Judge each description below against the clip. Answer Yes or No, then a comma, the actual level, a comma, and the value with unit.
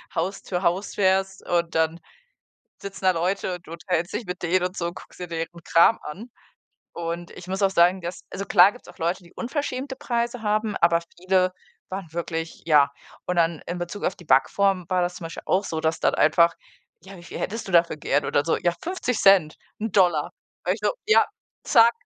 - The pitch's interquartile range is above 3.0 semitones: No, average, 2.7 semitones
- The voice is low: No, medium, 180 Hz